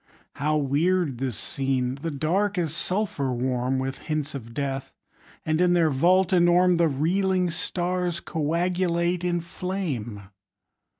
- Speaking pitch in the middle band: Yes, medium, 165 Hz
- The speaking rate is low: Yes, slow, 130 wpm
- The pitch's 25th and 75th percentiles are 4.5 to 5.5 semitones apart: Yes, average, 4.8 semitones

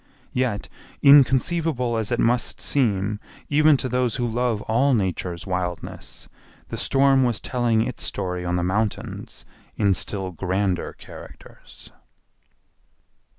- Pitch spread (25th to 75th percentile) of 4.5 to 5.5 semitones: Yes, average, 5.0 semitones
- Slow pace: Yes, slow, 120 wpm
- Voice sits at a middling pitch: No, low, 115 Hz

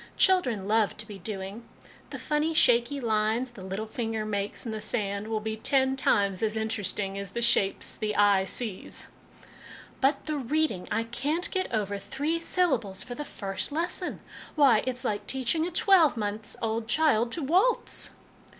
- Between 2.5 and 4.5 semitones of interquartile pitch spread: No, wide, 5.6 semitones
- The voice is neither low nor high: No, high, 225 Hz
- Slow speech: No, average, 170 wpm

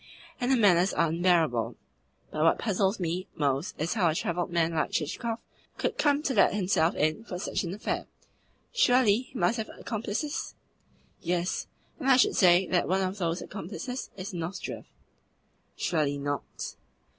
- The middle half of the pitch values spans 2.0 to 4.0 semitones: No, average, 5.0 semitones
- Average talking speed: Yes, average, 160 wpm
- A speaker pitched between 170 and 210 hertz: Yes, medium, 185 Hz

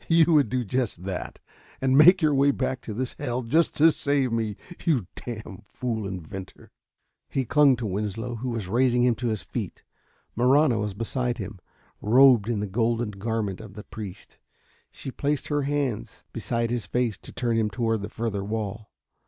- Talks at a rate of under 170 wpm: No, average, 180 wpm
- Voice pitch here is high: No, low, 115 Hz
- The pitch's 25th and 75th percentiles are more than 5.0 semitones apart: No, average, 3.8 semitones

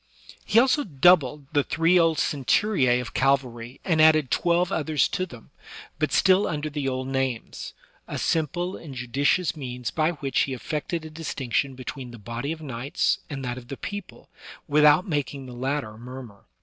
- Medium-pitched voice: Yes, medium, 145 Hz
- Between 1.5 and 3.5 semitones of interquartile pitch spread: No, average, 4.1 semitones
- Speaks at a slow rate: No, average, 175 wpm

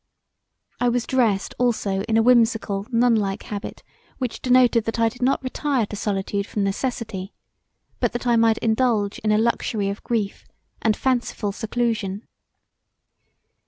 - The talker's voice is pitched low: No, high, 225 Hz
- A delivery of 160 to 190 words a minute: No, average, 145 wpm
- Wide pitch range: No, average, 3.0 semitones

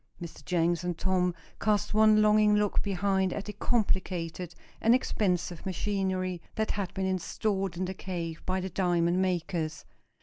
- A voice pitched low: No, medium, 185 Hz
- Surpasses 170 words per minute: No, average, 155 wpm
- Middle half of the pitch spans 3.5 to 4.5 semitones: No, narrow, 2.6 semitones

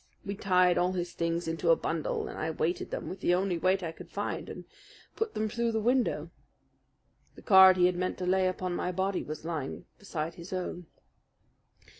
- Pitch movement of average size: No, narrow, 2.2 semitones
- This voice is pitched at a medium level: Yes, medium, 180 Hz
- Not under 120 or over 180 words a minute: No, average, 200 wpm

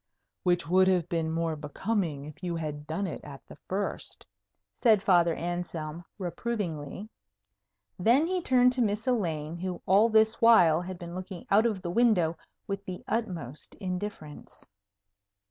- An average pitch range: Yes, average, 4.6 semitones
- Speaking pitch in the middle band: Yes, medium, 180 Hz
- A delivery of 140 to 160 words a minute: Yes, average, 150 wpm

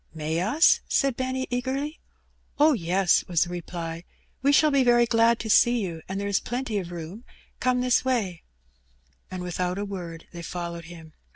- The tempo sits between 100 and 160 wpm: No, average, 185 wpm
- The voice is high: Yes, high, 200 Hz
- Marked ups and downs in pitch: Yes, wide, 6.4 semitones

